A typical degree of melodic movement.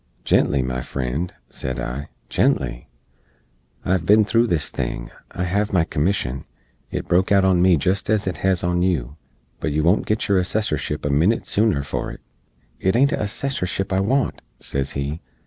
No: wide, 5.8 semitones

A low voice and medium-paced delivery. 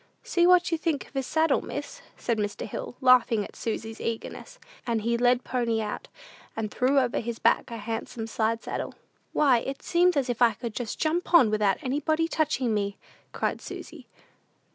No: high, 245 Hz; average, 185 wpm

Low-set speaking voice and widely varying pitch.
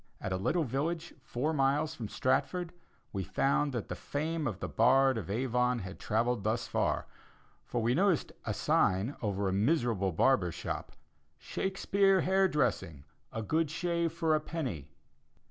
Yes: low, 130 Hz; wide, 7.1 semitones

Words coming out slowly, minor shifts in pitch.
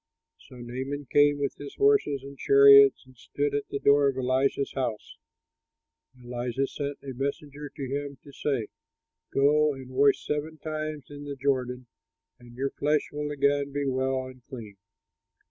No: average, 165 wpm; narrow, 1.8 semitones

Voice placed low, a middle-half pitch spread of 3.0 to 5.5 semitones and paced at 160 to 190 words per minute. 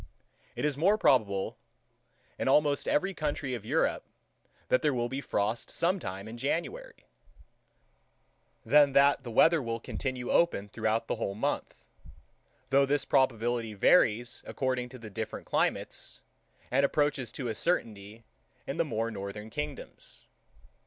No: low, 125 Hz; average, 4.6 semitones; average, 140 wpm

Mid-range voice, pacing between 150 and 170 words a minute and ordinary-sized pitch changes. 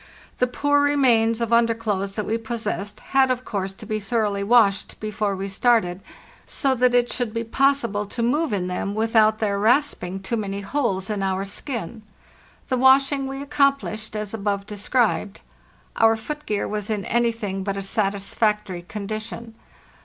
No: high, 220 Hz; average, 160 wpm; average, 3.4 semitones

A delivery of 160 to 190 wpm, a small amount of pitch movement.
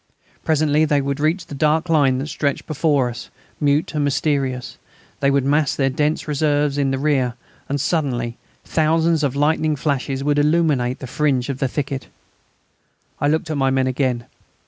Yes: average, 170 wpm; narrow, 2.3 semitones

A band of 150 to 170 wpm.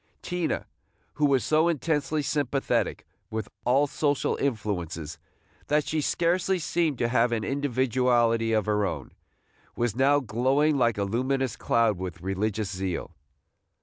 No: slow, 135 wpm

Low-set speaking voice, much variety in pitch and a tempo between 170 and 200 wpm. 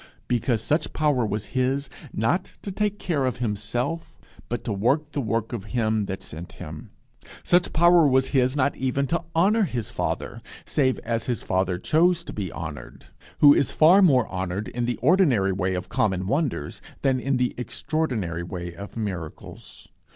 Yes: low, 125 Hz; wide, 6.6 semitones; average, 175 wpm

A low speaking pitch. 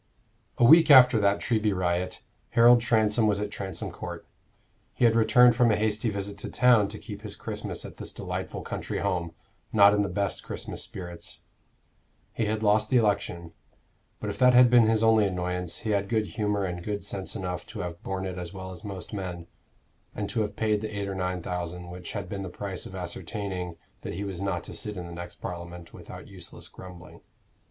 Yes: low, 100 Hz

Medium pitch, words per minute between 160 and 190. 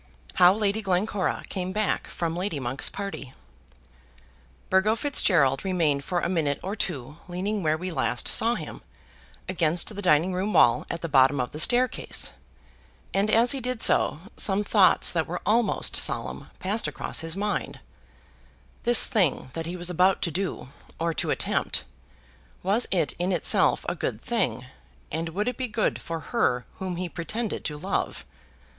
Yes: medium, 180 Hz; average, 165 wpm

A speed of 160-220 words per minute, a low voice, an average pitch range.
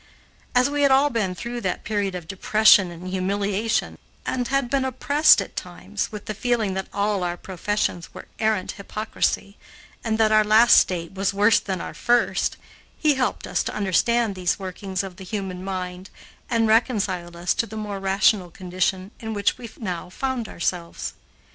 No: average, 175 wpm; high, 200 Hz; average, 3.5 semitones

